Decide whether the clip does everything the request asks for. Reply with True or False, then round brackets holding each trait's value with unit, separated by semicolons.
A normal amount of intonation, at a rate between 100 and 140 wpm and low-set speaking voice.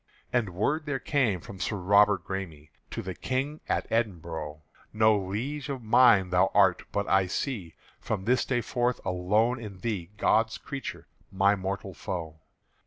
False (4.6 semitones; 160 wpm; 100 Hz)